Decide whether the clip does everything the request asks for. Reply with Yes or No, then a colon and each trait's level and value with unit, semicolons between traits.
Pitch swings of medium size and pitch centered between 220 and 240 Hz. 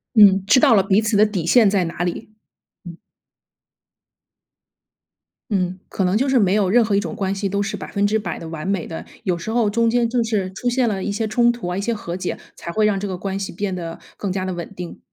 No: average, 3.0 semitones; high, 200 Hz